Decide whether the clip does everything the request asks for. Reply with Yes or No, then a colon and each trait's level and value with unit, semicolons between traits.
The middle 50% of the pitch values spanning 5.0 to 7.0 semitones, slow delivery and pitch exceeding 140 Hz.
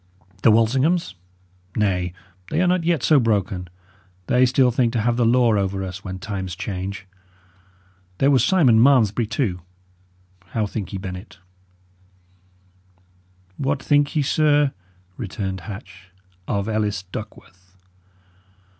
No: average, 5.3 semitones; slow, 125 wpm; low, 110 Hz